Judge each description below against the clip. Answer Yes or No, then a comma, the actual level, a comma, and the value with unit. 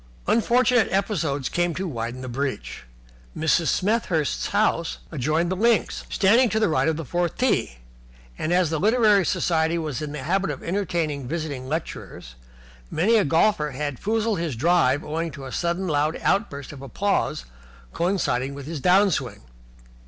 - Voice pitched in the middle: Yes, medium, 165 Hz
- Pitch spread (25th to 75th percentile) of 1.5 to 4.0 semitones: No, wide, 5.5 semitones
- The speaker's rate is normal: Yes, average, 160 wpm